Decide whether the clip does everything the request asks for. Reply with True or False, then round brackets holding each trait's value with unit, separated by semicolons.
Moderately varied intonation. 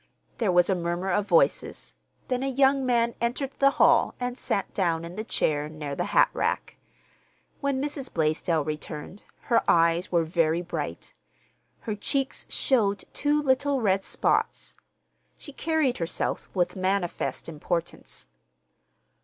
False (7.6 semitones)